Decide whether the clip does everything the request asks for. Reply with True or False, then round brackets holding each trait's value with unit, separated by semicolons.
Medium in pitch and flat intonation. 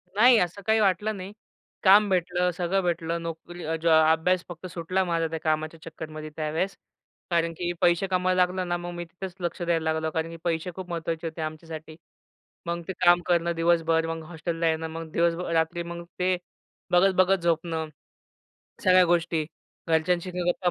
True (170 Hz; 1.8 semitones)